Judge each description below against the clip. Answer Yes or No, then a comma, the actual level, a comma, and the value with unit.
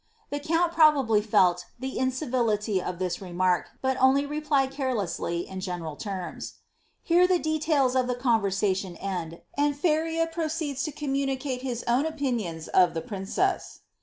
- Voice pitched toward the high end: Yes, very high, 255 Hz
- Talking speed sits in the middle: Yes, average, 145 wpm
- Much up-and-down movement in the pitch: Yes, wide, 7.4 semitones